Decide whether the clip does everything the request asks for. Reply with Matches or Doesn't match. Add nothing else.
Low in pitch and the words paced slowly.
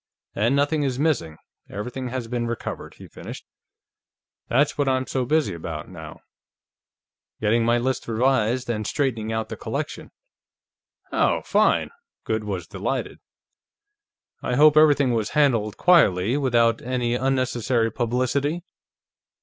Matches